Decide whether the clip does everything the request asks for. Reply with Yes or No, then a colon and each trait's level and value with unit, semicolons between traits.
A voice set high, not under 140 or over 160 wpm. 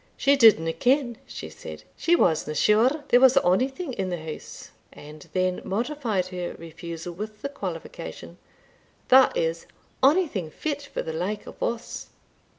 Yes: high, 215 Hz; average, 150 wpm